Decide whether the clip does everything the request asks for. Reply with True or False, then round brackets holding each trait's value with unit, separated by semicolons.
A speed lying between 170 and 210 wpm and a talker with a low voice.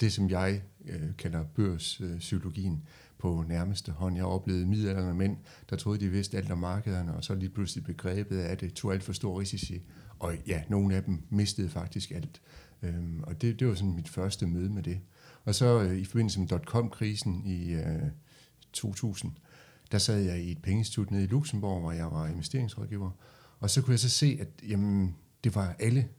True (195 wpm; 95 Hz)